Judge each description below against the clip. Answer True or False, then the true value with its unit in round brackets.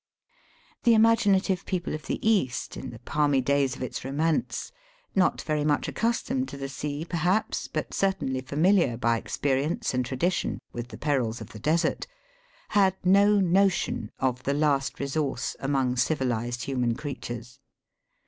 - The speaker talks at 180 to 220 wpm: False (160 wpm)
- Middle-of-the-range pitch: True (145 Hz)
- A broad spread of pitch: True (6.5 semitones)